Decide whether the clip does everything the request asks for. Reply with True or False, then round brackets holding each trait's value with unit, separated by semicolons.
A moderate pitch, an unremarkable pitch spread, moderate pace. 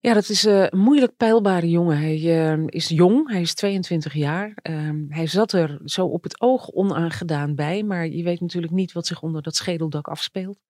True (175 Hz; 3.3 semitones; 190 wpm)